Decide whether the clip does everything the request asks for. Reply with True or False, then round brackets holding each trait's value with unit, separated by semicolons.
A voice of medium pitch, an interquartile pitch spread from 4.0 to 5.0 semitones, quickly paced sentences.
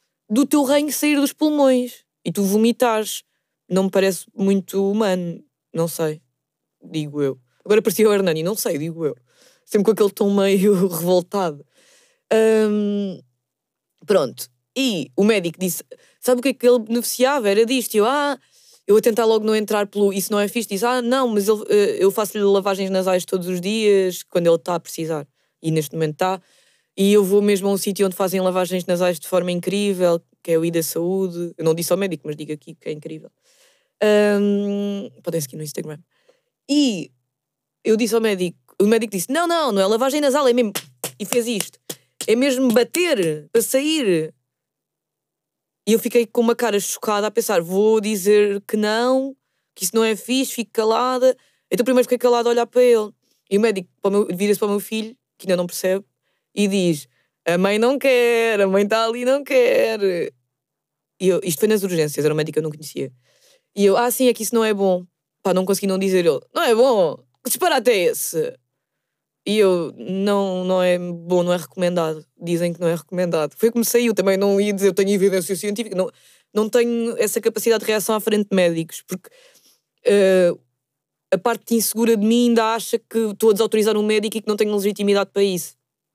False (205 Hz; 4.6 semitones; 205 wpm)